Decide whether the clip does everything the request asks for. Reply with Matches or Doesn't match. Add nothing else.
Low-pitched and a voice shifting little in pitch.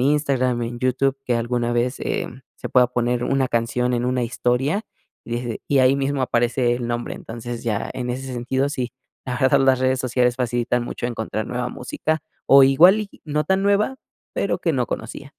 Matches